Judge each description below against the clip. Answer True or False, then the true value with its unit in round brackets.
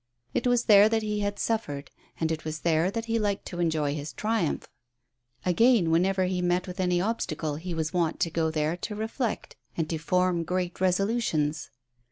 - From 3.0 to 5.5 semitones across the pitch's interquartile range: True (4.5 semitones)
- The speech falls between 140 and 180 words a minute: False (190 wpm)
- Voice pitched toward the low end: False (180 Hz)